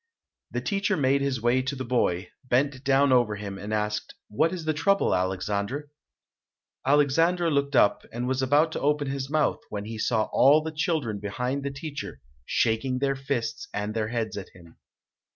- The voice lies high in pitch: No, low, 130 Hz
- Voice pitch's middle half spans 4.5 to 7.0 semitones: Yes, average, 4.9 semitones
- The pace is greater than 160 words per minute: Yes, average, 180 wpm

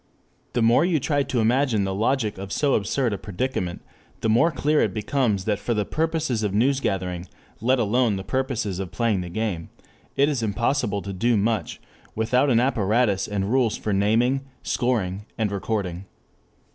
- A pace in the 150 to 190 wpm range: Yes, average, 170 wpm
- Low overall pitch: Yes, low, 110 Hz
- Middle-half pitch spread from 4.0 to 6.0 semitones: Yes, average, 4.5 semitones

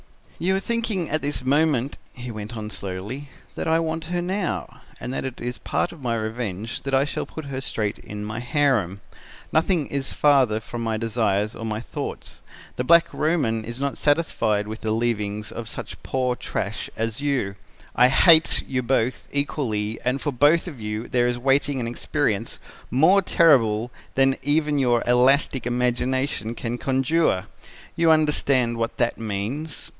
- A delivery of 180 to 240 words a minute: No, average, 170 wpm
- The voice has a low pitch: Yes, low, 125 Hz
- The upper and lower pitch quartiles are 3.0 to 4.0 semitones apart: No, average, 4.5 semitones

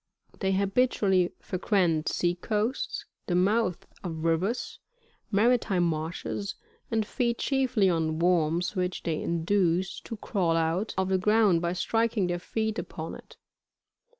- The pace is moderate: No, slow, 130 wpm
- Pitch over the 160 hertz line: Yes, high, 190 Hz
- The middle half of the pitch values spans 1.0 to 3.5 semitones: No, average, 3.9 semitones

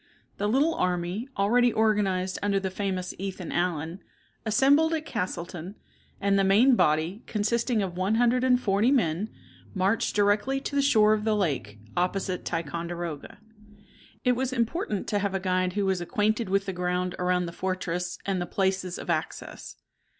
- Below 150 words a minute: No, average, 165 wpm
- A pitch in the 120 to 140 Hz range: No, high, 195 Hz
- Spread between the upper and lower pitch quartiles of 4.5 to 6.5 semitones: No, average, 3.5 semitones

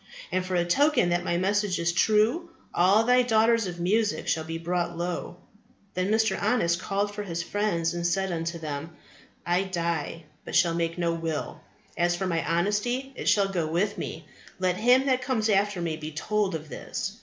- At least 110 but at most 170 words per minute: No, average, 190 wpm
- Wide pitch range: No, average, 3.8 semitones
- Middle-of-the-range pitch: Yes, medium, 180 Hz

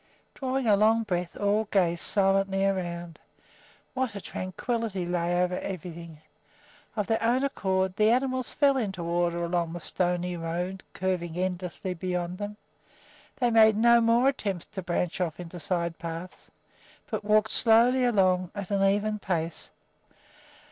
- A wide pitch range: No, average, 3.8 semitones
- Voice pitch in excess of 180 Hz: Yes, high, 190 Hz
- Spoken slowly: No, average, 145 wpm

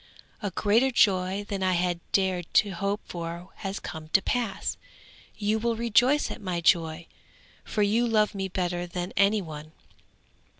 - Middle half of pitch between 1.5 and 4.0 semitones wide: Yes, average, 3.3 semitones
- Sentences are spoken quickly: No, average, 160 wpm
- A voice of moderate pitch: No, high, 195 Hz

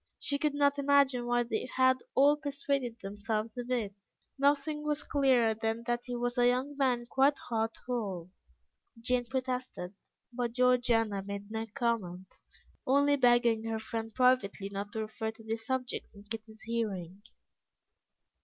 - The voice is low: No, high, 240 Hz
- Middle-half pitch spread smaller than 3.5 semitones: Yes, average, 2.9 semitones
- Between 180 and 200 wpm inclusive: No, average, 150 wpm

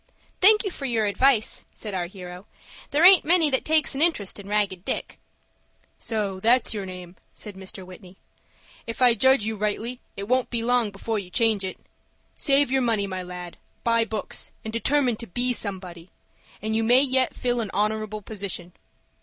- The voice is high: Yes, high, 220 Hz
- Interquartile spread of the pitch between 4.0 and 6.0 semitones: Yes, average, 4.4 semitones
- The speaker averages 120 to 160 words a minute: No, average, 180 wpm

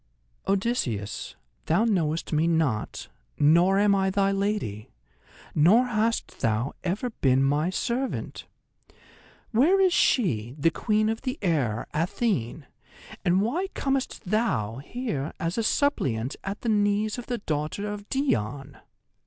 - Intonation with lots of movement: Yes, wide, 7.6 semitones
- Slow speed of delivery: Yes, slow, 130 wpm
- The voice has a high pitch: Yes, high, 195 Hz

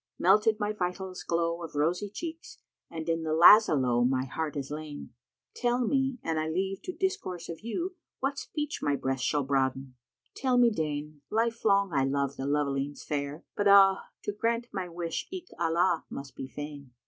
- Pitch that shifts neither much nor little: No, wide, 6.7 semitones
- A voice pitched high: No, medium, 170 Hz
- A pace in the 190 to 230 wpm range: Yes, average, 195 wpm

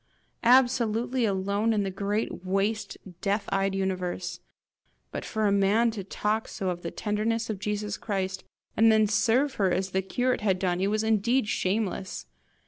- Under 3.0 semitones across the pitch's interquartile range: Yes, narrow, 2.5 semitones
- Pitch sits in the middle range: No, high, 210 Hz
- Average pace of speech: Yes, average, 165 wpm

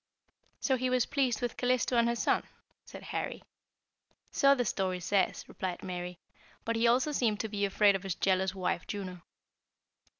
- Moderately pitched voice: No, high, 210 Hz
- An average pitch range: Yes, average, 4.7 semitones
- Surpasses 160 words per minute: Yes, average, 170 wpm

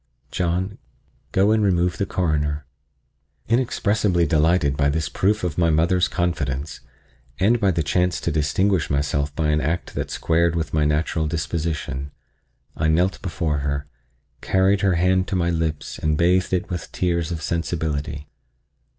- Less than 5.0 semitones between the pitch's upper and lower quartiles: Yes, average, 3.2 semitones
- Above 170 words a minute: No, average, 150 wpm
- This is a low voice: Yes, very low, 85 Hz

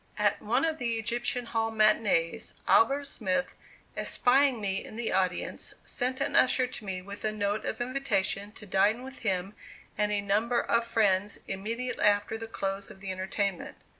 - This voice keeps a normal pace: Yes, average, 170 wpm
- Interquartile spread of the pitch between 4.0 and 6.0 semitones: No, average, 3.5 semitones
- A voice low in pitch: No, high, 215 Hz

